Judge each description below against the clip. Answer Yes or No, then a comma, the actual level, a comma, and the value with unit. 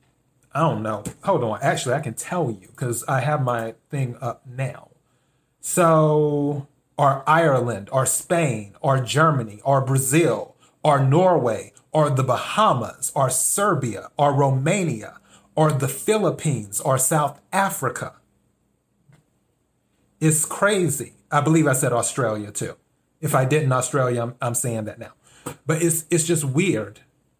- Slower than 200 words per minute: Yes, average, 140 wpm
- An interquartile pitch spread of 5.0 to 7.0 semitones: No, average, 4.1 semitones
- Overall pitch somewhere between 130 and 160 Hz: Yes, medium, 140 Hz